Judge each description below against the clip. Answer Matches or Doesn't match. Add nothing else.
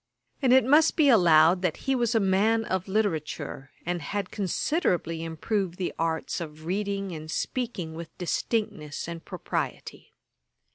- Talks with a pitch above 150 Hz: Matches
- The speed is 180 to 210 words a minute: Doesn't match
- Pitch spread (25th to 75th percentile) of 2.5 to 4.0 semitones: Doesn't match